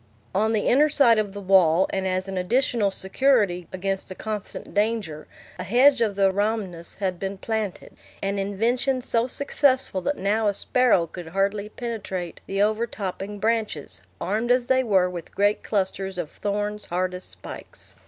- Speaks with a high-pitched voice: Yes, high, 205 Hz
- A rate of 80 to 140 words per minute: No, average, 165 wpm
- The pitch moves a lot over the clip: No, average, 3.3 semitones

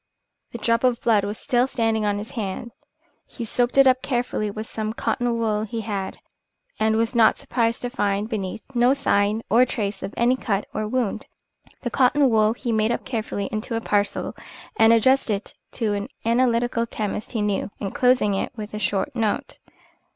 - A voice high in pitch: Yes, high, 225 Hz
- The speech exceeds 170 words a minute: Yes, average, 185 wpm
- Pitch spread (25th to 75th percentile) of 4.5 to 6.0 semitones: No, narrow, 2.4 semitones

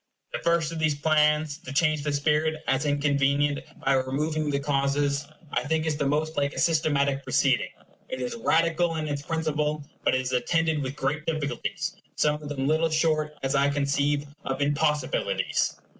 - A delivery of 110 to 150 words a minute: No, average, 175 wpm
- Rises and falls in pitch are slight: Yes, narrow, 1.9 semitones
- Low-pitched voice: No, medium, 150 Hz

